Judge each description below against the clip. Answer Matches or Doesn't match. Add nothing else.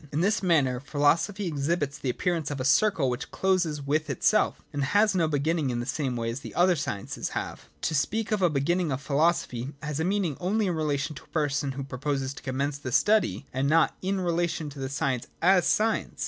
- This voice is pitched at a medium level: Matches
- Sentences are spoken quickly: Matches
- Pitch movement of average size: Matches